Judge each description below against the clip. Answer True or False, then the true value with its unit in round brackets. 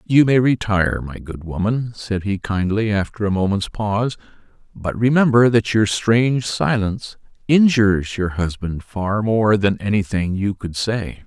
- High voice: False (105 Hz)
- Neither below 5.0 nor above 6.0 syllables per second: False (4.5 syllables/s)